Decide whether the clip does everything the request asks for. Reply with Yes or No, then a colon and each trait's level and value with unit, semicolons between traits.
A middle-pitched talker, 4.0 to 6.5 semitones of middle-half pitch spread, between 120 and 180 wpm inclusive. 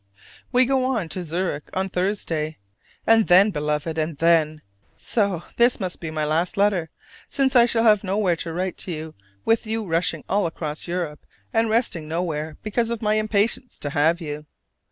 Yes: medium, 180 Hz; average, 5.2 semitones; average, 175 wpm